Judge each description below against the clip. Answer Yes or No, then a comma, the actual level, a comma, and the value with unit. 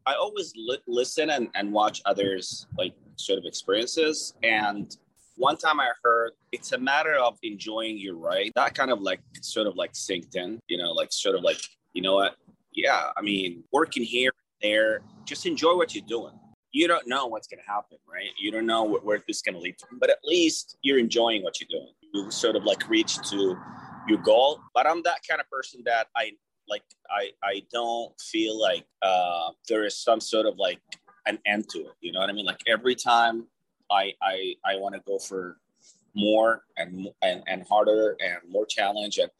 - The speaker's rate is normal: No, fast, 210 wpm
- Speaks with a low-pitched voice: Yes, low, 115 Hz